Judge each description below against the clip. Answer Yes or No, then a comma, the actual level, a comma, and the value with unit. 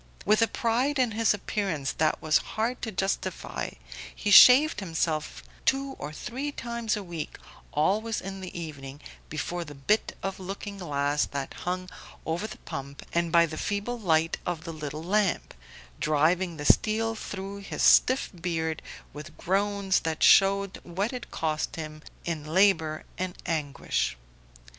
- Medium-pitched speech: Yes, medium, 180 Hz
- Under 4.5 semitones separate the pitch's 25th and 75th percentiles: No, average, 4.9 semitones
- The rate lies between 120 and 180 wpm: Yes, average, 155 wpm